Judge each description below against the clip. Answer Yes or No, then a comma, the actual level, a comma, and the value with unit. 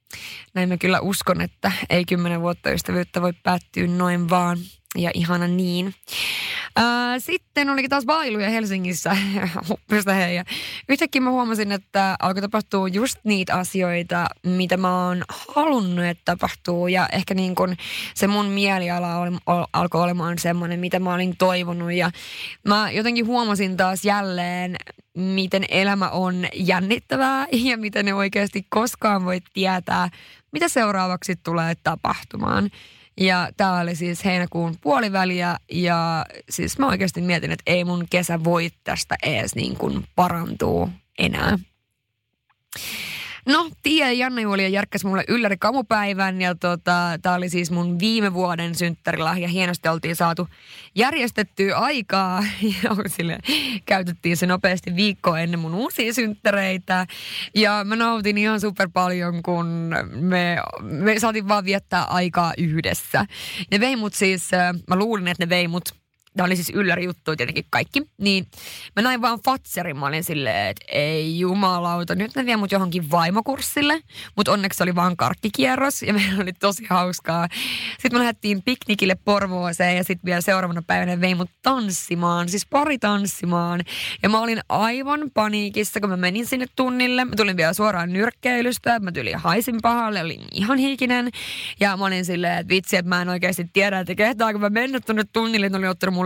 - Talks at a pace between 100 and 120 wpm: No, average, 150 wpm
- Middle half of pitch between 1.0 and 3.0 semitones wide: No, average, 3.5 semitones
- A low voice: No, medium, 185 Hz